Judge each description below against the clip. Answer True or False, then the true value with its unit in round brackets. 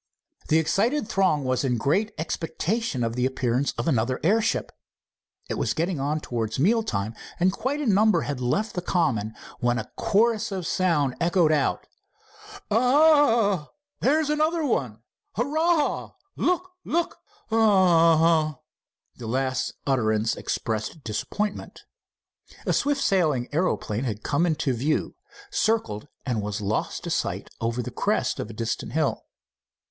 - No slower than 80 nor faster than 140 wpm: True (135 wpm)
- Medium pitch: True (160 Hz)